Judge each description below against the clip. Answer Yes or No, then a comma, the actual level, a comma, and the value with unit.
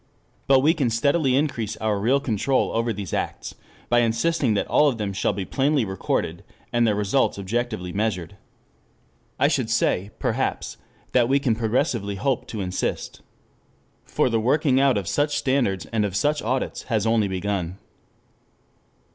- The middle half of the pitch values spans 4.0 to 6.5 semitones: Yes, average, 4.8 semitones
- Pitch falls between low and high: No, low, 115 Hz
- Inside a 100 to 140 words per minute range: No, average, 160 wpm